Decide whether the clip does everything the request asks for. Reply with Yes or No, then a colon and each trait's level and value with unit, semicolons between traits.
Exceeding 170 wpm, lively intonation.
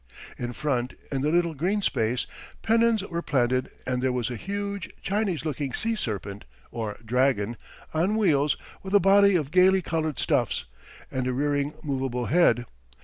No: average, 160 wpm; wide, 7.1 semitones